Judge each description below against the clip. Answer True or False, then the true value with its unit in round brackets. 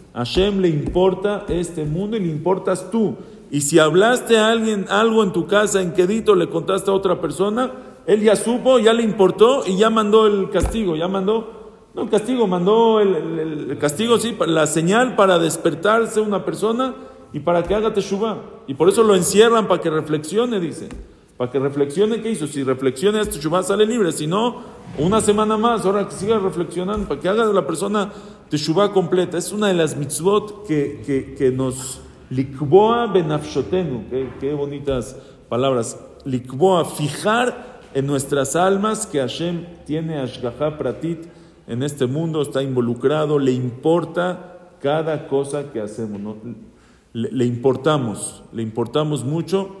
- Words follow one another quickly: False (165 wpm)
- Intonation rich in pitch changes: True (6.3 semitones)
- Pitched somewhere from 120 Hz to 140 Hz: False (180 Hz)